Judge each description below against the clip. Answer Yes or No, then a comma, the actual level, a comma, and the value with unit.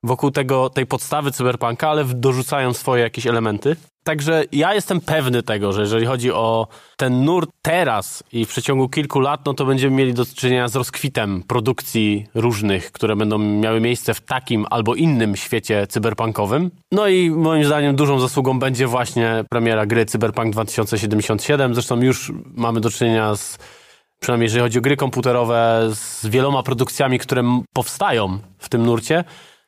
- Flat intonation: No, average, 3.5 semitones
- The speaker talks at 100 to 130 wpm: No, fast, 160 wpm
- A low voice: Yes, low, 125 Hz